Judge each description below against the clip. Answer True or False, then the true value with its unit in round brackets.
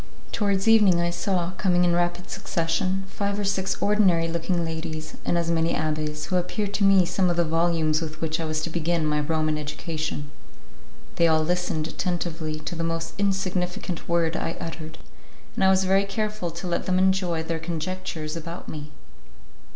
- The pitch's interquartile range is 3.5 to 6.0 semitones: False (2.7 semitones)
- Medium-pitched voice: True (170 Hz)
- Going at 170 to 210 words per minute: True (180 wpm)